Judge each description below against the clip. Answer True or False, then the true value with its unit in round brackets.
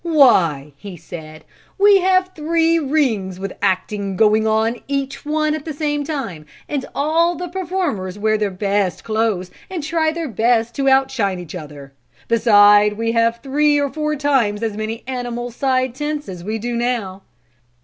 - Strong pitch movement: True (6.4 semitones)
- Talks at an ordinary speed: True (170 wpm)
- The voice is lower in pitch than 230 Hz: False (235 Hz)